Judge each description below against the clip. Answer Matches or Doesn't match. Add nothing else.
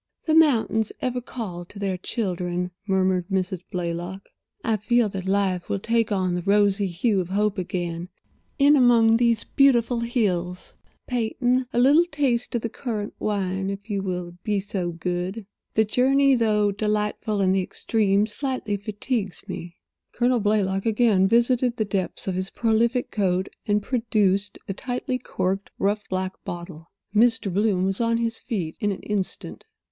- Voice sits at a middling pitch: Doesn't match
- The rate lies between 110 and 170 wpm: Matches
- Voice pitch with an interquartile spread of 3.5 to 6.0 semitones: Matches